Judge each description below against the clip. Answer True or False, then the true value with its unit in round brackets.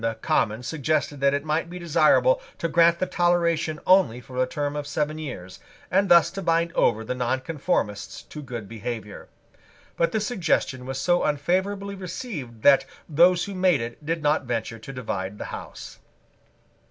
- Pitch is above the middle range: False (150 Hz)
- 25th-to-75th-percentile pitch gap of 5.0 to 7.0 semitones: True (5.6 semitones)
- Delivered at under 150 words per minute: False (185 wpm)